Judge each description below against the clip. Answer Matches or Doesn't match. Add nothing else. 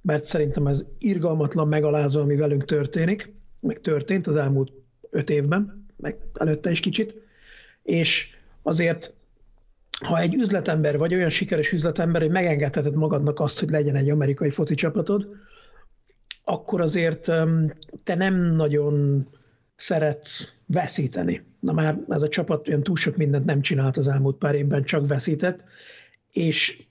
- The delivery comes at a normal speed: Matches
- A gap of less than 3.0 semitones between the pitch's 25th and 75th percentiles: Doesn't match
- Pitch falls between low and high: Matches